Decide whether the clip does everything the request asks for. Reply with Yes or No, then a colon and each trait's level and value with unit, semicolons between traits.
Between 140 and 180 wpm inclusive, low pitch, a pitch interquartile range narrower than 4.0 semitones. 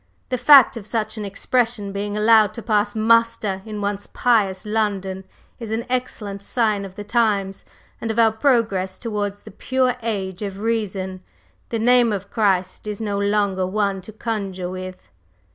No: average, 165 wpm; high, 210 Hz; narrow, 2.5 semitones